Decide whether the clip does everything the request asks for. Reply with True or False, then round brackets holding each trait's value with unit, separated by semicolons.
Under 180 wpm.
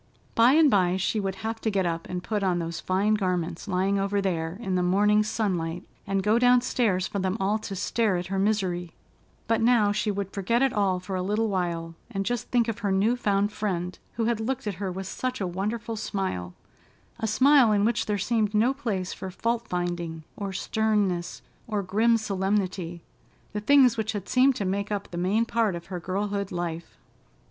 False (200 wpm)